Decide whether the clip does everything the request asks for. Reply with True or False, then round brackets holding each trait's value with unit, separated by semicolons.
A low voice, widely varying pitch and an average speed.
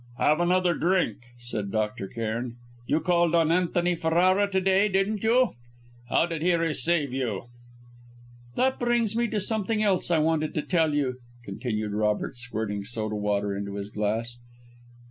False (155 Hz; 8.9 semitones; 155 wpm)